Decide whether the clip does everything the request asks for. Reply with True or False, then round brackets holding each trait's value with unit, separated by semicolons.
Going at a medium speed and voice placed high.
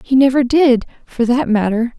True (180 wpm; 250 Hz)